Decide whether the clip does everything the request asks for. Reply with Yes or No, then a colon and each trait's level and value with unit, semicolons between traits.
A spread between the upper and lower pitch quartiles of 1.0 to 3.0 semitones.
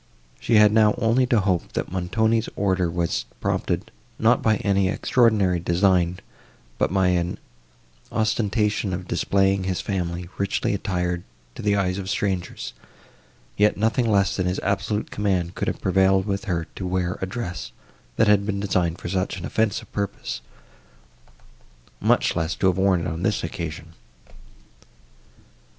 Yes: narrow, 2.6 semitones